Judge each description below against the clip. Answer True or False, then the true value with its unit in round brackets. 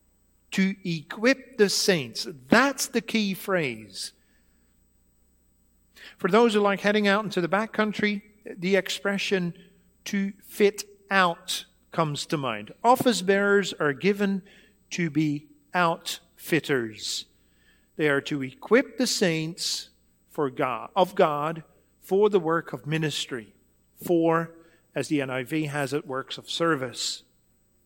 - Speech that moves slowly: True (125 wpm)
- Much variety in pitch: True (6.9 semitones)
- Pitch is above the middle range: False (170 Hz)